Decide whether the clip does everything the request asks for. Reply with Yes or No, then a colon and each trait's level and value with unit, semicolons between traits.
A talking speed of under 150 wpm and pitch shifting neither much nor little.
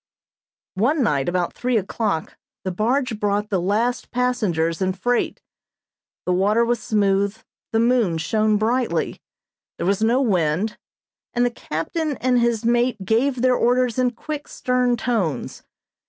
Yes: average, 140 wpm; average, 4.2 semitones